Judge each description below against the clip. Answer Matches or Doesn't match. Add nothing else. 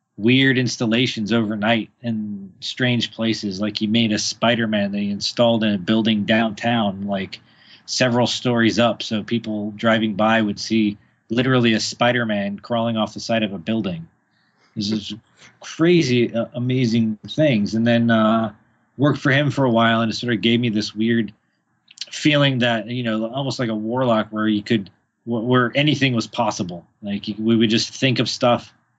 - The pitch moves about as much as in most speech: Doesn't match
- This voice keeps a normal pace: Matches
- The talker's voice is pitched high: Doesn't match